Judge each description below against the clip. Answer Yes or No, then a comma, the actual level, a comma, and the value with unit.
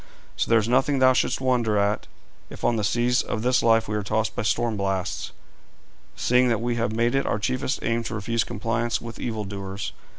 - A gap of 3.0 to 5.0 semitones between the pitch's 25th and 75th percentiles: No, narrow, 2.5 semitones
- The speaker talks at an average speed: No, fast, 210 wpm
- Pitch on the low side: Yes, low, 115 Hz